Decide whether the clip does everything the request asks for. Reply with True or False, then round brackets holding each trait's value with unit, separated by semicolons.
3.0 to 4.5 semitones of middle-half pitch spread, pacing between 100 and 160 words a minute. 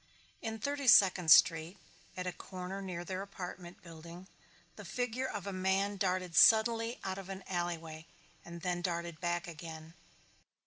False (2.5 semitones; 150 wpm)